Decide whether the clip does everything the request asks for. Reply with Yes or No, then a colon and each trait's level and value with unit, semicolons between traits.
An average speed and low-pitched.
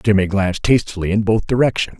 Yes: average, 180 wpm; low, 105 Hz